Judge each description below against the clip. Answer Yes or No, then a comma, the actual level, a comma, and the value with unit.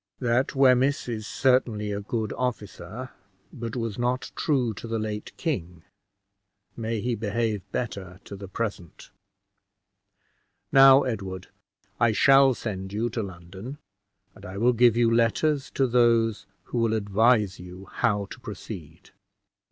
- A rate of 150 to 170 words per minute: No, slow, 135 wpm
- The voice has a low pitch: Yes, low, 115 Hz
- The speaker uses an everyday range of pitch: Yes, average, 3.5 semitones